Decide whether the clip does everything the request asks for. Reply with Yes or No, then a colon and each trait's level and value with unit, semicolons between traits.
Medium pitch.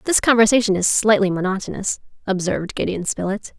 No: high, 205 Hz